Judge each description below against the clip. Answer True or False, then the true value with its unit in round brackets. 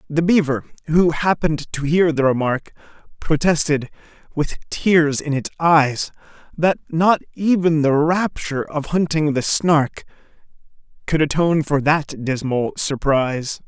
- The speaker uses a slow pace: True (125 wpm)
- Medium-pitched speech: True (150 Hz)